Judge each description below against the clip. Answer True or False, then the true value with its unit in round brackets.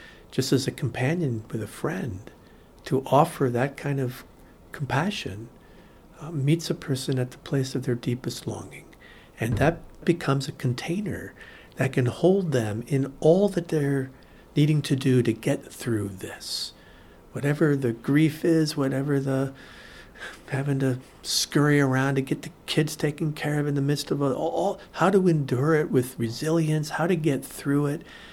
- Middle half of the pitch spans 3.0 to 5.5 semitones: True (3.3 semitones)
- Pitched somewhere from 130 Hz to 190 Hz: True (140 Hz)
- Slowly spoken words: False (165 wpm)